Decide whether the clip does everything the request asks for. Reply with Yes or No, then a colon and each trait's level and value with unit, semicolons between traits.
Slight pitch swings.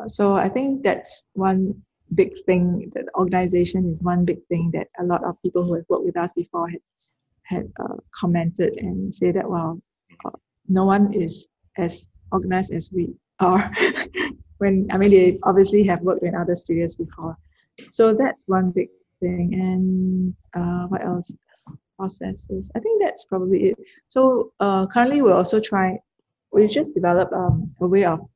Yes: narrow, 1.8 semitones